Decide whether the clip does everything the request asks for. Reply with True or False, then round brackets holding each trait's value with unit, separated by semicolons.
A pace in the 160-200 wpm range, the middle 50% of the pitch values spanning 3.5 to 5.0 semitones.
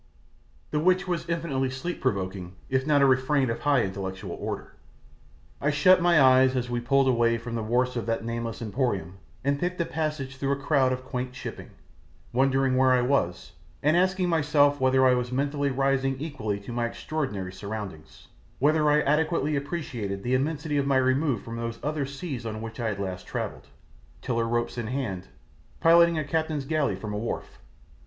True (185 wpm; 4.1 semitones)